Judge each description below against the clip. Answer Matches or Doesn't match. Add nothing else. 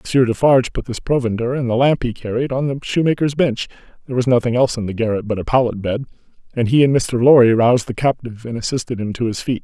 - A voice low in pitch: Matches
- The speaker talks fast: Matches